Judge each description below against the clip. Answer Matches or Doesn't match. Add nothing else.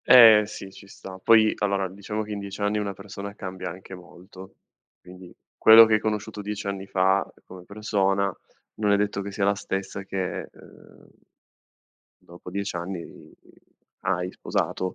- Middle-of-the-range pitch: Doesn't match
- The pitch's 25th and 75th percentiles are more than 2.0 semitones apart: Doesn't match